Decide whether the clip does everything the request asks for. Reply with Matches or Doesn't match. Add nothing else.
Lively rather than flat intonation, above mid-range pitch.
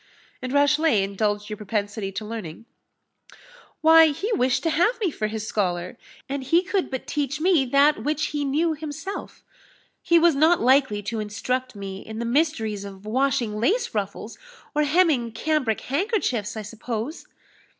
Matches